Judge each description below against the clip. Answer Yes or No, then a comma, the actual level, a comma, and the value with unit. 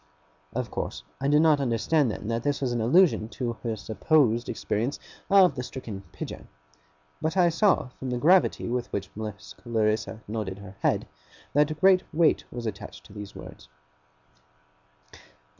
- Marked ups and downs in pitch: Yes, wide, 5.8 semitones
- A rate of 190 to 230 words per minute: No, average, 160 wpm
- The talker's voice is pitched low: Yes, low, 120 Hz